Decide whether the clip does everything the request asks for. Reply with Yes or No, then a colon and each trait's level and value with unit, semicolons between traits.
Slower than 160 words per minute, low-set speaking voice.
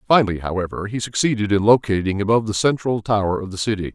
No: average, 200 wpm; low, 105 Hz